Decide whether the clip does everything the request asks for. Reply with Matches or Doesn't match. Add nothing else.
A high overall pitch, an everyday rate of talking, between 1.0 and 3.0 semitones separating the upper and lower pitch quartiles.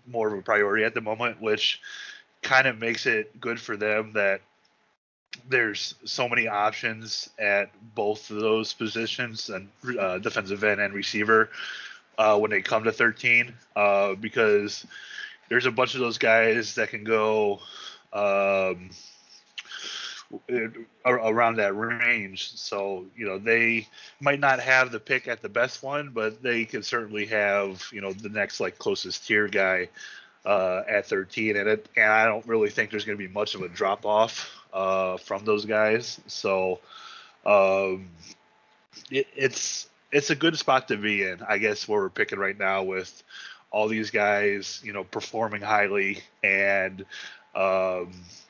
Doesn't match